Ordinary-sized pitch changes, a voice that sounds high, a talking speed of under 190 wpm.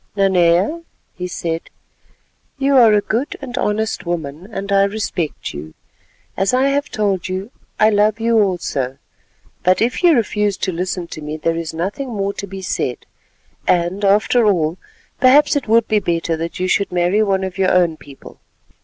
Yes: average, 4.0 semitones; high, 195 Hz; average, 175 wpm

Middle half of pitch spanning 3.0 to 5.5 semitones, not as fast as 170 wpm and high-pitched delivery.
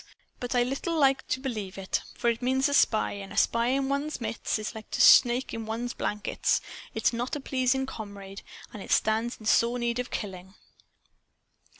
No: average, 3.3 semitones; fast, 205 wpm; high, 240 Hz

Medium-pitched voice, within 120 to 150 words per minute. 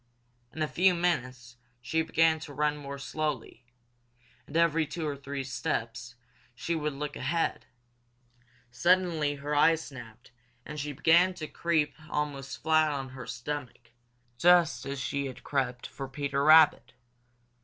Yes: medium, 145 Hz; average, 145 wpm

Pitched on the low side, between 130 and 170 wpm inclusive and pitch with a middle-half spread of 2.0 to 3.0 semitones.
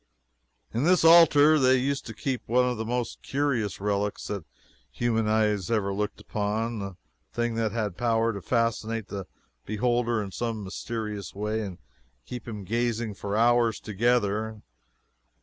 Yes: low, 115 Hz; average, 150 wpm; narrow, 2.6 semitones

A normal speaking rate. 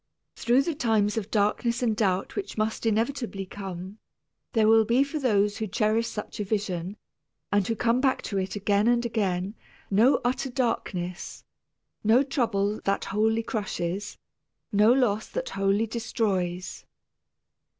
Yes: average, 145 wpm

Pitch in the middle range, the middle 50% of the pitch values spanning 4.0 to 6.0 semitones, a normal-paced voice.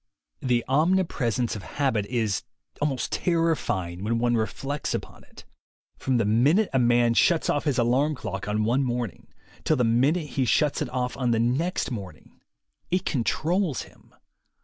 No: low, 125 Hz; average, 4.3 semitones; average, 160 wpm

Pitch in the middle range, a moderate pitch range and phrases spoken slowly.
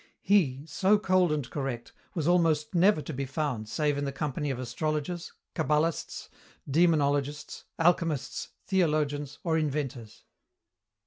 Yes: medium, 150 Hz; average, 3.0 semitones; slow, 125 wpm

